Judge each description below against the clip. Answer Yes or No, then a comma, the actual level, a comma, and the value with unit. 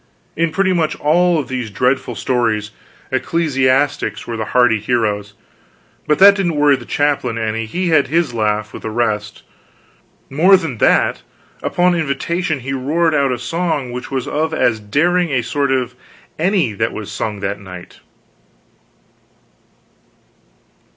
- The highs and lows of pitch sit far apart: Yes, wide, 6.2 semitones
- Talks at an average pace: Yes, average, 145 wpm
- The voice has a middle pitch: No, low, 130 Hz